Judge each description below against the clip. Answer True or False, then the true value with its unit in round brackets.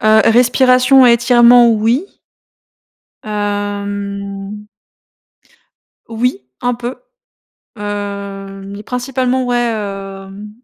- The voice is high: True (215 Hz)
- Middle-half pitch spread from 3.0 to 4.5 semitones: True (3.4 semitones)